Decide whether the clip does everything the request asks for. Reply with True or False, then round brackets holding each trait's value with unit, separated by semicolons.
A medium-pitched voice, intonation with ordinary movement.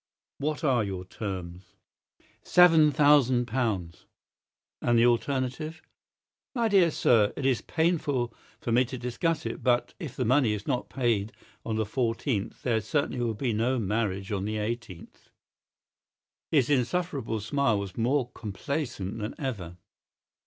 False (120 Hz; 4.8 semitones)